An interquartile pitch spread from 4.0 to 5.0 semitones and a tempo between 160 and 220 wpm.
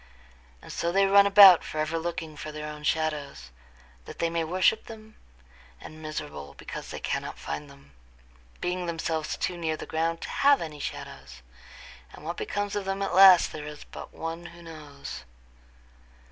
No: average, 3.4 semitones; average, 170 wpm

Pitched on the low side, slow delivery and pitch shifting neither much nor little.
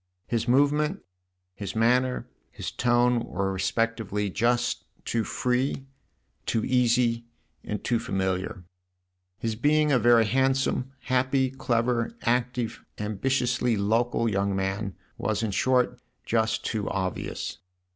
Yes: low, 115 Hz; slow, 115 wpm; average, 3.0 semitones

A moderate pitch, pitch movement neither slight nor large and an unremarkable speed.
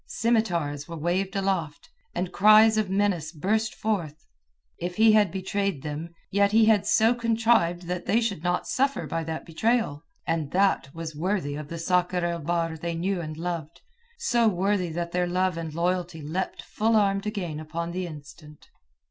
Yes: medium, 180 Hz; average, 3.8 semitones; average, 175 wpm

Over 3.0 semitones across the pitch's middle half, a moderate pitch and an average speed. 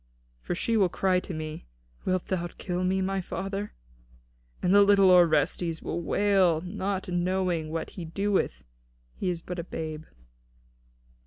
No: narrow, 2.5 semitones; medium, 180 Hz; average, 155 wpm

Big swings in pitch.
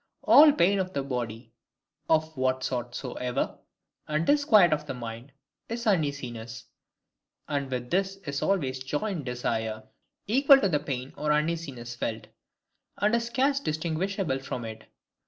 Yes: wide, 7.4 semitones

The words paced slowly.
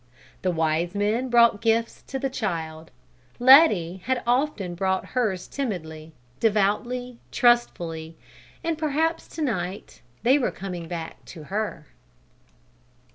Yes: slow, 120 wpm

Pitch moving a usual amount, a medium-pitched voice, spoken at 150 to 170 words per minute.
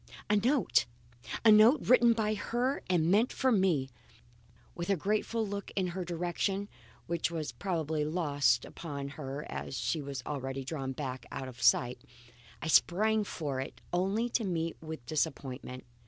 No: wide, 6.6 semitones; medium, 170 Hz; average, 155 wpm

